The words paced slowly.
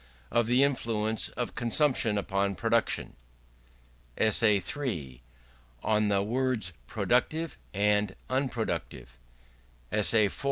Yes: slow, 95 wpm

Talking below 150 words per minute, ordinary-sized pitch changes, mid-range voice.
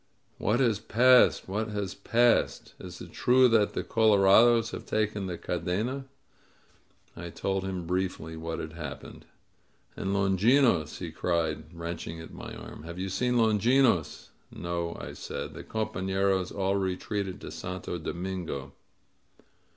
No: slow, 135 wpm; average, 4.2 semitones; very low, 95 Hz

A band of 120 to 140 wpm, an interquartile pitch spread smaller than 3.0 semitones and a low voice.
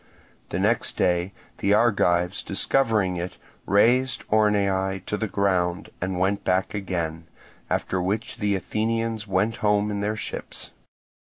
Yes: slow, 135 wpm; narrow, 2.6 semitones; low, 100 Hz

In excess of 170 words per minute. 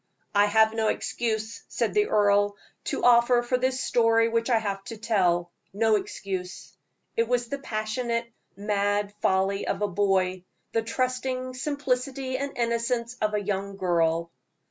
No: average, 150 wpm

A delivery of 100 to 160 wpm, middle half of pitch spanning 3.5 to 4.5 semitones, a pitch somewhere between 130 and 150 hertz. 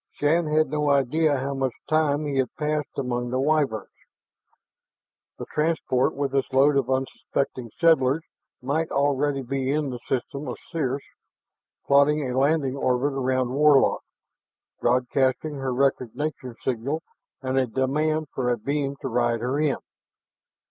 No: average, 140 wpm; narrow, 2.5 semitones; low, 135 Hz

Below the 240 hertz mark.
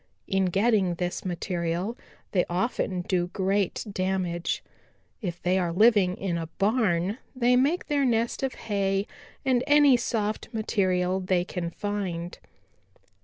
Yes: high, 190 Hz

